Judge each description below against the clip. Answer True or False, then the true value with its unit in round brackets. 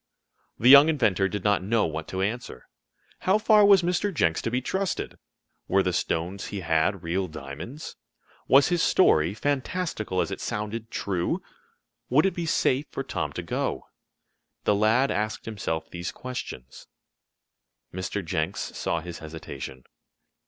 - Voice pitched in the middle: False (105 Hz)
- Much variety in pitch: True (8.3 semitones)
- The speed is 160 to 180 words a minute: False (150 wpm)